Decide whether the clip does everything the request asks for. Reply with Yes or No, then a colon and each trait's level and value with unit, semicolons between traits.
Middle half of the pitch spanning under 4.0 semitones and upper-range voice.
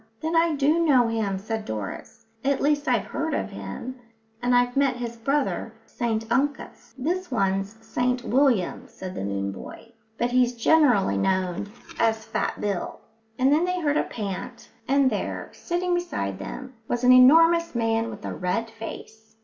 No: average, 5.0 semitones; high, 245 Hz